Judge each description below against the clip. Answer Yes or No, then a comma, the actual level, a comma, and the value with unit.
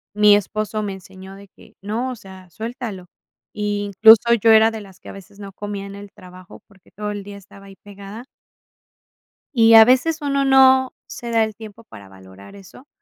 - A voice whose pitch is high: Yes, high, 205 Hz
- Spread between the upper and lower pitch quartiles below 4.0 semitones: Yes, narrow, 2.5 semitones